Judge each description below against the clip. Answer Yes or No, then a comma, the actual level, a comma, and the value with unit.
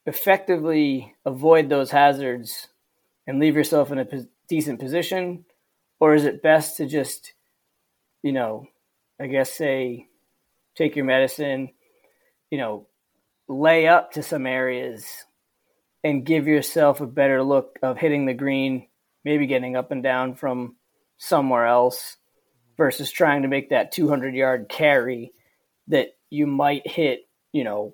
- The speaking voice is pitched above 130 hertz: Yes, medium, 140 Hz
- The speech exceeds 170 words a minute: No, average, 140 wpm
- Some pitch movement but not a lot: Yes, average, 3.1 semitones